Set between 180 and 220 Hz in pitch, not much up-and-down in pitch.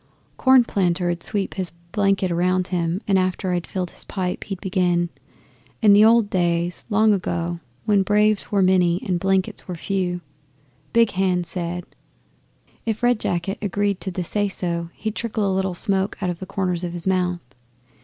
Yes: medium, 185 Hz; narrow, 2.3 semitones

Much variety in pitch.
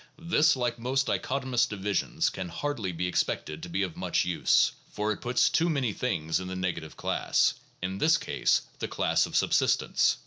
Yes: wide, 6.7 semitones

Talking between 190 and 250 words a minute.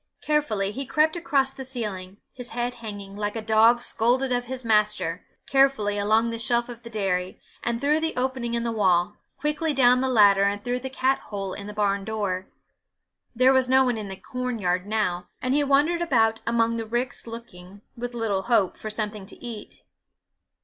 Yes: average, 195 wpm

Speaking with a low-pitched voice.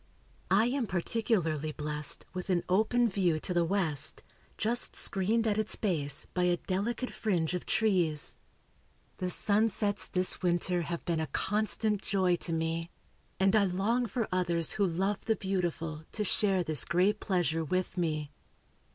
No: medium, 185 Hz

